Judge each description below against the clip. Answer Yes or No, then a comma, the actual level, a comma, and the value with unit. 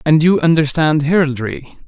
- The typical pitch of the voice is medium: Yes, medium, 155 Hz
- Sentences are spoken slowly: Yes, slow, 130 wpm